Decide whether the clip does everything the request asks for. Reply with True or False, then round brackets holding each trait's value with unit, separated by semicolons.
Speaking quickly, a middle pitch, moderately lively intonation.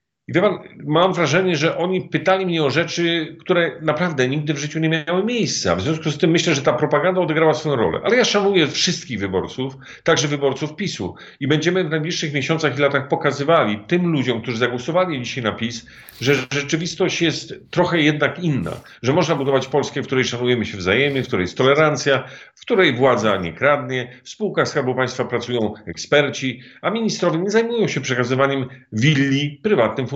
True (180 wpm; 150 Hz; 4.4 semitones)